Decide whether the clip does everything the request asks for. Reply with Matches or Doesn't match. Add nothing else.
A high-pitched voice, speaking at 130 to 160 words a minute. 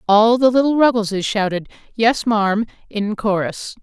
Matches